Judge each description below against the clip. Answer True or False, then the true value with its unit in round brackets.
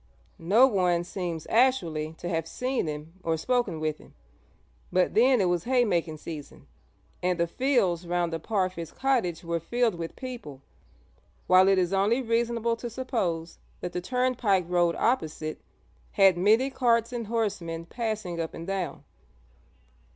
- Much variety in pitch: True (5.8 semitones)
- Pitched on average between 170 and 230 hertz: True (185 Hz)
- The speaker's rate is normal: True (150 wpm)